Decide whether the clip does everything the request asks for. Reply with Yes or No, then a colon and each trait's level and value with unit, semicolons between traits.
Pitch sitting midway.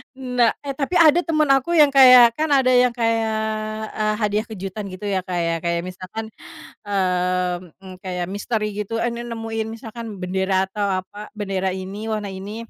No: high, 215 Hz